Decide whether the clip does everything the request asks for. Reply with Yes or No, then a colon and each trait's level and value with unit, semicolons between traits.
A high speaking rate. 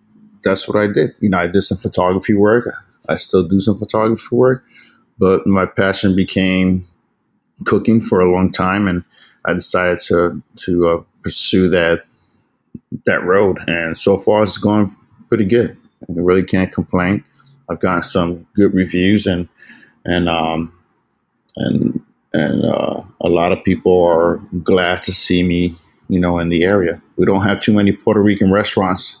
No: average, 165 wpm